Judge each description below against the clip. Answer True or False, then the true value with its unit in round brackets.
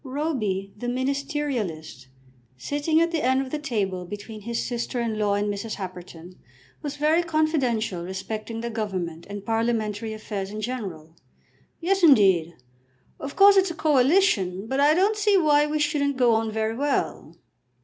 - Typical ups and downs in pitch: False (6.5 semitones)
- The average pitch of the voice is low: False (235 Hz)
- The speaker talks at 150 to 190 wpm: True (160 wpm)